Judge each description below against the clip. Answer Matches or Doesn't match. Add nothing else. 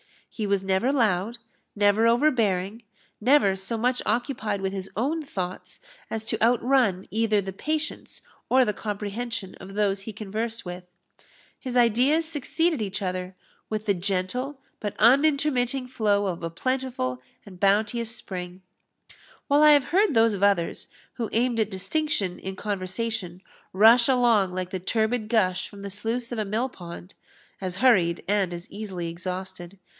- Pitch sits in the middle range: Doesn't match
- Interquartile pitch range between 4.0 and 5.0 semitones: Matches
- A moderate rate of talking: Matches